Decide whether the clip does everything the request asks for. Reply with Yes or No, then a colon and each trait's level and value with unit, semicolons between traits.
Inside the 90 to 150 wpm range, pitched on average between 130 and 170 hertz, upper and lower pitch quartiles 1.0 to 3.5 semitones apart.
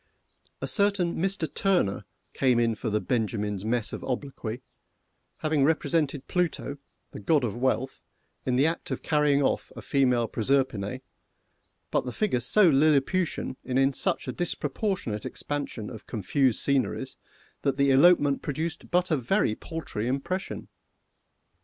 No: average, 140 wpm; low, 135 Hz; average, 4.6 semitones